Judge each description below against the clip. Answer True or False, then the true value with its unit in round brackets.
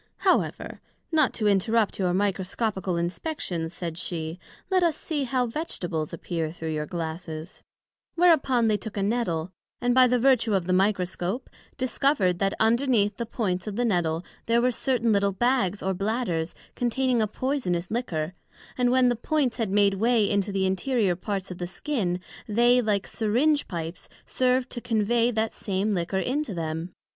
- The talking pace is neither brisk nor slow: True (165 wpm)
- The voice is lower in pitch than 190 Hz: False (210 Hz)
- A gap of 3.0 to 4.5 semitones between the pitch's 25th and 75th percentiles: False (5.3 semitones)